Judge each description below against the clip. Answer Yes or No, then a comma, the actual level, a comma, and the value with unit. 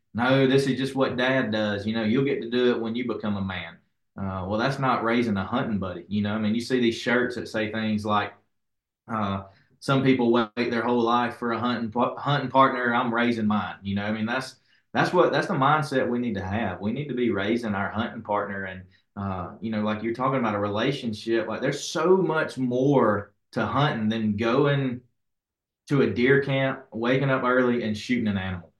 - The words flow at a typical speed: No, fast, 220 wpm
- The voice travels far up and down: No, average, 3.6 semitones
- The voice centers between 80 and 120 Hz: Yes, low, 115 Hz